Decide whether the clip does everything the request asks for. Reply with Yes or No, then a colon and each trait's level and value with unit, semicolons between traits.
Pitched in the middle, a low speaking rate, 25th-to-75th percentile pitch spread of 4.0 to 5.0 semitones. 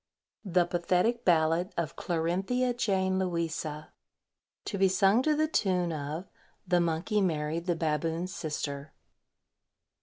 No: medium, 175 Hz; slow, 120 wpm; average, 3.0 semitones